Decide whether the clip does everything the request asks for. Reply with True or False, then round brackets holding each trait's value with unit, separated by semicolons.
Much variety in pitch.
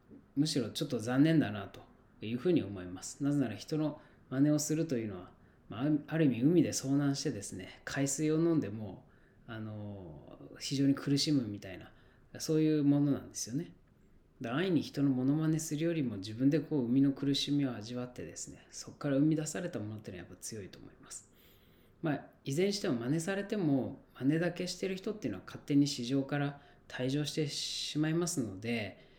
False (4.4 semitones)